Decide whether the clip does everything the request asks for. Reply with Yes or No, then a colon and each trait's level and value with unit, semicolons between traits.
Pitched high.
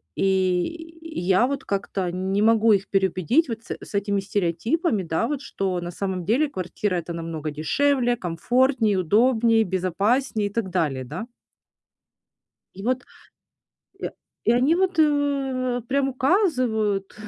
Yes: high, 215 Hz